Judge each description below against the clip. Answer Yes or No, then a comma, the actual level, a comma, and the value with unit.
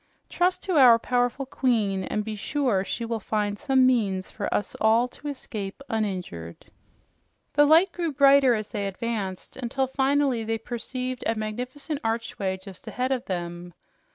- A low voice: No, high, 230 Hz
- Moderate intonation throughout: Yes, average, 4.5 semitones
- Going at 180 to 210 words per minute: No, average, 155 wpm